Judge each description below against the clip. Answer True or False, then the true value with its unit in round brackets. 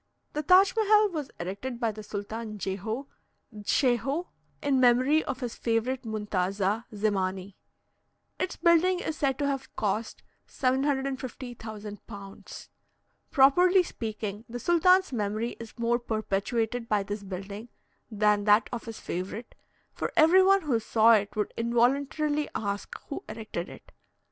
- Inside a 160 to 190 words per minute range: False (135 wpm)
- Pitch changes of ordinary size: True (4.9 semitones)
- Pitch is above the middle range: True (230 Hz)